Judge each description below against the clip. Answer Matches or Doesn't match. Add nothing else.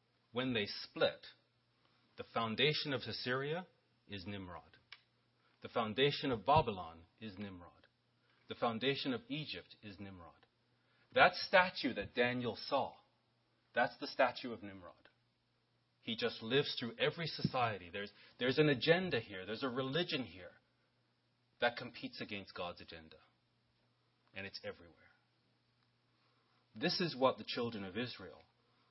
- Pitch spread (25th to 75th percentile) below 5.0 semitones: Doesn't match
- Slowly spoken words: Matches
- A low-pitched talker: Matches